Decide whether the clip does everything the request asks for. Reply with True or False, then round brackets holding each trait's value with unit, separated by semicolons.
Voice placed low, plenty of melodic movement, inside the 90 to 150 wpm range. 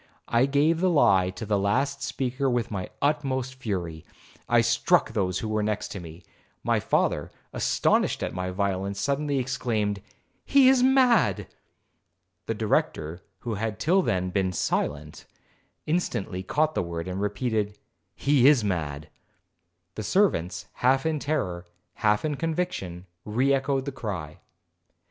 True (110 Hz; 7.1 semitones; 140 wpm)